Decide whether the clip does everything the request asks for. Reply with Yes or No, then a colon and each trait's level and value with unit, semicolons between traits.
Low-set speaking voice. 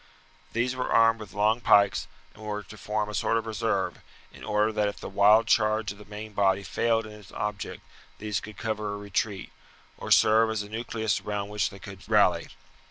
Yes: low, 105 Hz